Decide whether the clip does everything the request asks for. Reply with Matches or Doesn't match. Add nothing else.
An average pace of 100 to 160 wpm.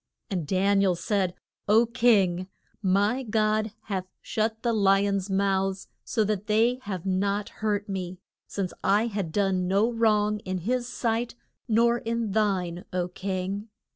Matches